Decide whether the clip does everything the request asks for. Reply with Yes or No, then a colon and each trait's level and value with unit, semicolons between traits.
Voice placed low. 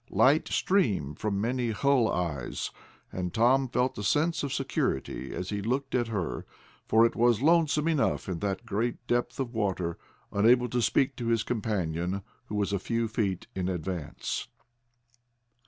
Yes: low, 115 Hz